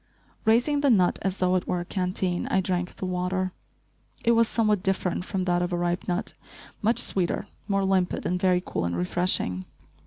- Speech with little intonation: Yes, narrow, 1.6 semitones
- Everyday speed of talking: Yes, average, 190 wpm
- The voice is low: No, medium, 185 Hz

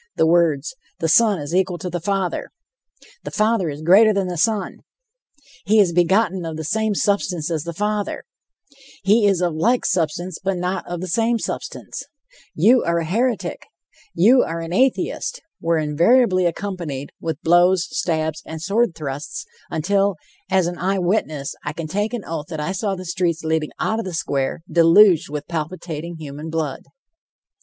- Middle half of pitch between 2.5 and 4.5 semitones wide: Yes, average, 3.9 semitones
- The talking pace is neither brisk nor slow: Yes, average, 170 wpm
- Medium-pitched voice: Yes, medium, 175 Hz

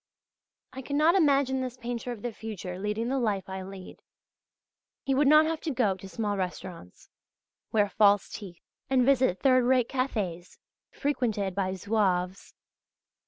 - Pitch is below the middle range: No, high, 220 Hz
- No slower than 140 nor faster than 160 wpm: Yes, average, 150 wpm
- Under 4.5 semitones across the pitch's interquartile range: No, wide, 5.4 semitones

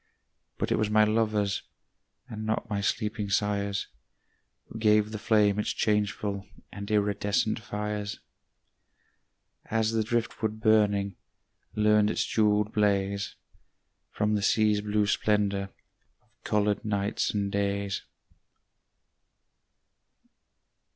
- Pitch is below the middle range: Yes, low, 105 Hz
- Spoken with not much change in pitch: Yes, narrow, 1.0 semitones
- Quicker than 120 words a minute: No, slow, 105 wpm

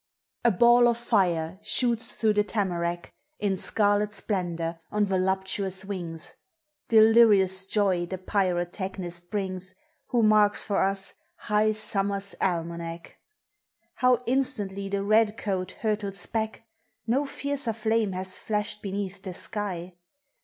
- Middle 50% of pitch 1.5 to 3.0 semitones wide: Yes, average, 2.7 semitones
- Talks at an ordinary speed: No, slow, 120 wpm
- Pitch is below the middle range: No, high, 200 Hz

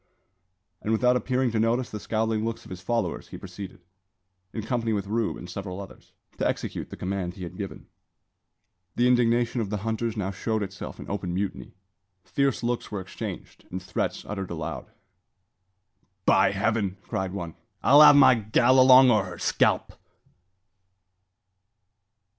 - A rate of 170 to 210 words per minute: No, average, 155 wpm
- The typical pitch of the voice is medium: No, low, 110 Hz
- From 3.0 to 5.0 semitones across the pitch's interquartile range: Yes, average, 3.7 semitones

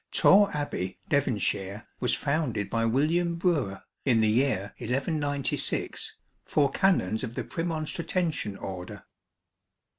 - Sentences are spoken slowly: Yes, slow, 115 wpm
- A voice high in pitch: No, low, 135 Hz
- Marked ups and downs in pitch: Yes, wide, 6.6 semitones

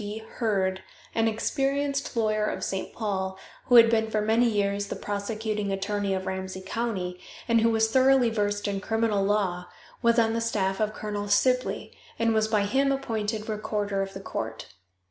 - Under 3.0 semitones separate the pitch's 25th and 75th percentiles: Yes, narrow, 2.4 semitones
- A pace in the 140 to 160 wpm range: No, average, 175 wpm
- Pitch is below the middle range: No, high, 215 Hz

